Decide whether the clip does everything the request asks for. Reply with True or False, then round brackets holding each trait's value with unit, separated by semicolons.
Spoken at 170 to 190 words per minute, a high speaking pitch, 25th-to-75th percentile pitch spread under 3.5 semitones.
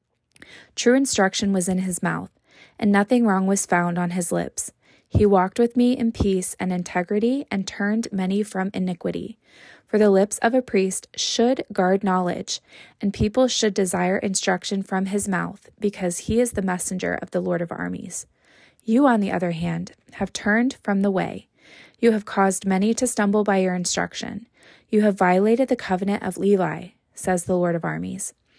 True (180 wpm; 195 Hz; 2.9 semitones)